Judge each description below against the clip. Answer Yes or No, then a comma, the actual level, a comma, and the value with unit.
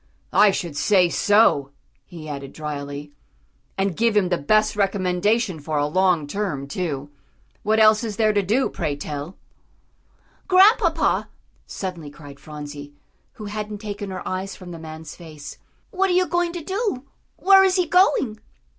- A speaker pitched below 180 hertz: No, high, 190 Hz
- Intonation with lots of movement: Yes, wide, 6.3 semitones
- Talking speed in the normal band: Yes, average, 155 wpm